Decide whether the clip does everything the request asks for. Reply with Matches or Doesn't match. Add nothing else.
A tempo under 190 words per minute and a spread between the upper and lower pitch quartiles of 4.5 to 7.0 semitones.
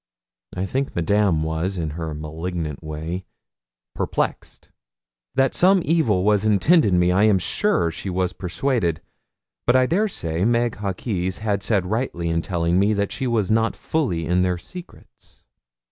Matches